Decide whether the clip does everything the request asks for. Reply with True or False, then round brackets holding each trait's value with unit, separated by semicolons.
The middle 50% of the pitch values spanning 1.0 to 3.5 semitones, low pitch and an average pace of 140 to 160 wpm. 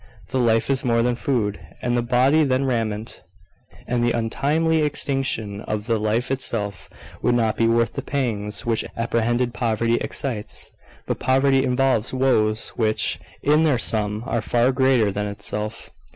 True (3.2 semitones; 120 Hz; 155 wpm)